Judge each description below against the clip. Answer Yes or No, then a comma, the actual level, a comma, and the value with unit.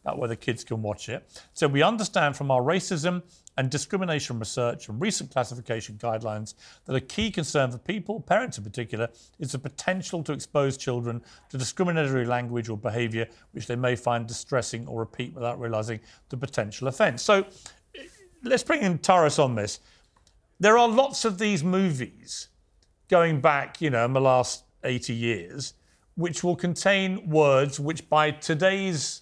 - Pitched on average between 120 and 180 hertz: Yes, low, 135 Hz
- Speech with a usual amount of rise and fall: No, wide, 7.1 semitones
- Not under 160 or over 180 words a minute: Yes, average, 165 wpm